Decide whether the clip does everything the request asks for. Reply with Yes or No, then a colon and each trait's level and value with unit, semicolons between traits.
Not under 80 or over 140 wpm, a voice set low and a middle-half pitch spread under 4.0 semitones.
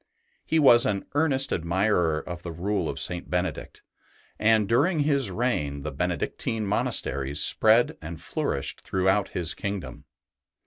No: slow, 135 wpm; low, 100 Hz; wide, 5.5 semitones